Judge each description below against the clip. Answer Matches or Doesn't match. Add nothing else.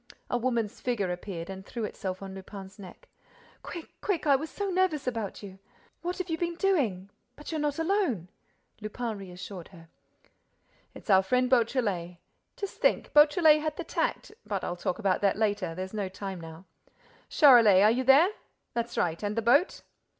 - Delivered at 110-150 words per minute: Doesn't match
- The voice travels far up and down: Matches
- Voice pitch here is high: Matches